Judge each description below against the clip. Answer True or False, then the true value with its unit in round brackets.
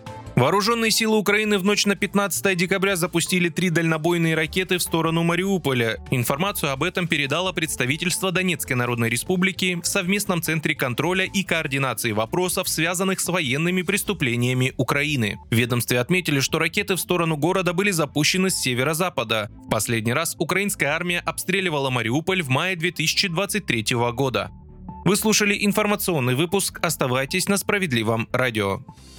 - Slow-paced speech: False (135 wpm)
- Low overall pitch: False (170 Hz)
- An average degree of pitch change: False (6.1 semitones)